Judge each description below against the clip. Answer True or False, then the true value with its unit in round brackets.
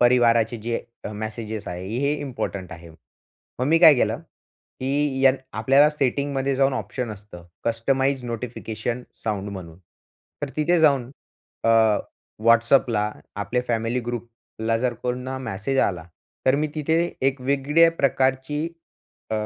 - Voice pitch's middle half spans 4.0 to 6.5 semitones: False (3.6 semitones)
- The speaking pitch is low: True (125 Hz)